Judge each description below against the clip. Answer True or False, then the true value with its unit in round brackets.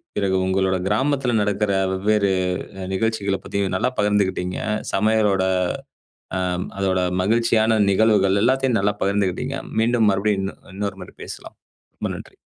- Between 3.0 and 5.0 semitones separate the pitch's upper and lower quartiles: False (2.5 semitones)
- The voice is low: True (105 Hz)